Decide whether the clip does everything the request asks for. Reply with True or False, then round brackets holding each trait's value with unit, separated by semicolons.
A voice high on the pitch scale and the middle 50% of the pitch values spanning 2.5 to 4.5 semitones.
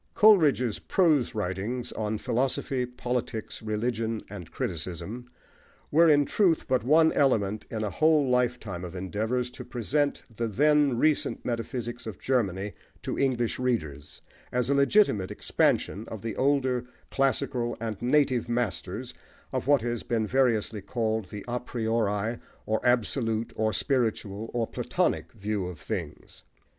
False (120 Hz; 3.3 semitones)